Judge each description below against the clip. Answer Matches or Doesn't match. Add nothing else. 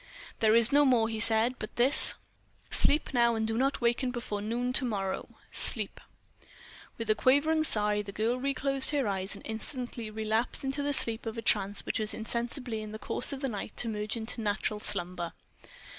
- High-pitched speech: Matches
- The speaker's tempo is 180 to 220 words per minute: Matches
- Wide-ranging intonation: Doesn't match